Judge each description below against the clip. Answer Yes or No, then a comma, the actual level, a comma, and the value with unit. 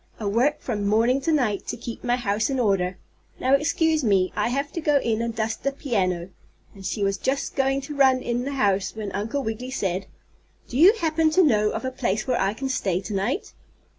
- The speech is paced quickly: Yes, fast, 225 wpm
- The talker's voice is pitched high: Yes, high, 240 Hz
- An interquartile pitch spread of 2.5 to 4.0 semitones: No, average, 5.2 semitones